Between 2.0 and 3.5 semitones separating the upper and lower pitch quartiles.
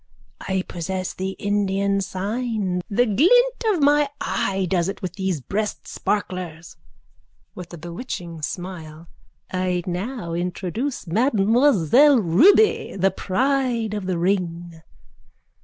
No: average, 4.9 semitones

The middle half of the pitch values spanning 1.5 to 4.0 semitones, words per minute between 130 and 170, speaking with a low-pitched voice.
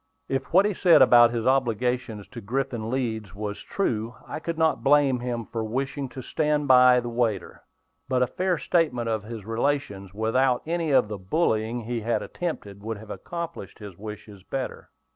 No: average, 3.7 semitones; average, 180 wpm; low, 120 Hz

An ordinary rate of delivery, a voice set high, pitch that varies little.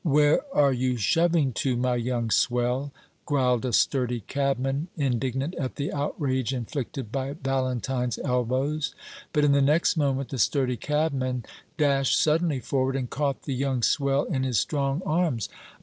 No: average, 150 wpm; low, 135 Hz; narrow, 2.3 semitones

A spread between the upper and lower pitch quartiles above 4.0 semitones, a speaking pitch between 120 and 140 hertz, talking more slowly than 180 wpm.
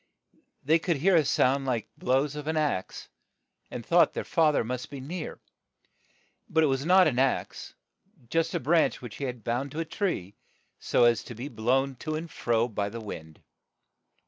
No: average, 4.7 semitones; low, 135 Hz; average, 190 wpm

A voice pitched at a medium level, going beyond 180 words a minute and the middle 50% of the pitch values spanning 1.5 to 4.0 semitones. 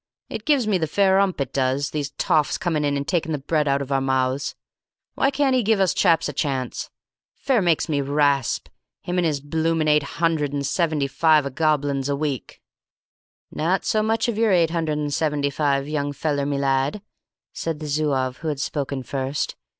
Yes: medium, 150 Hz; average, 200 wpm; average, 3.2 semitones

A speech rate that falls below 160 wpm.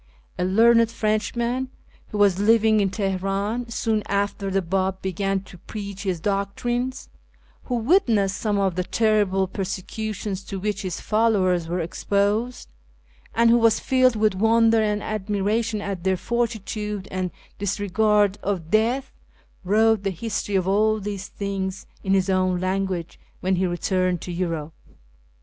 Yes: average, 145 wpm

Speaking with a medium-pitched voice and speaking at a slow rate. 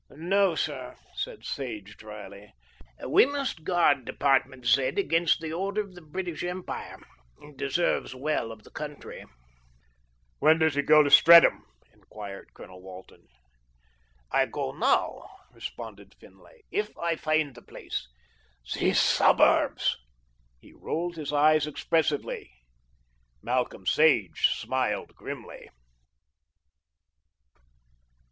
Yes: medium, 150 Hz; slow, 110 wpm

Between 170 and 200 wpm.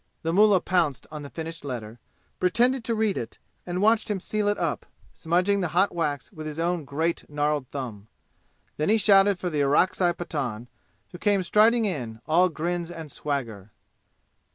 Yes: average, 175 wpm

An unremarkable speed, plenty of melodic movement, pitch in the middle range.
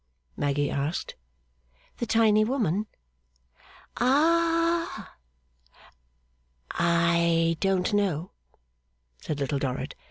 No: slow, 70 wpm; wide, 7.1 semitones; medium, 180 Hz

